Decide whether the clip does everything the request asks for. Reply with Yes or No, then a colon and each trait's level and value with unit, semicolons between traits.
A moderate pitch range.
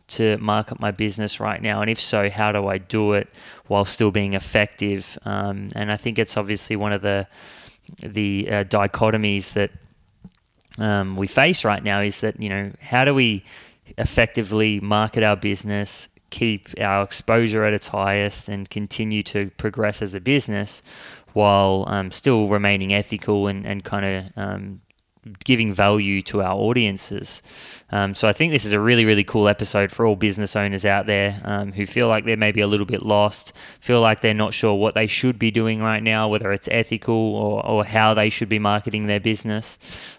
No: narrow, 1.5 semitones